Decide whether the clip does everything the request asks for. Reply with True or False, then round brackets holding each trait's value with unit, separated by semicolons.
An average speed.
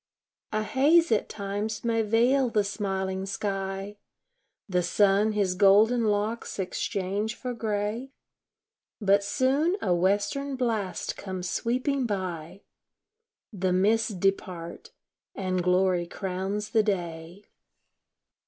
False (105 wpm)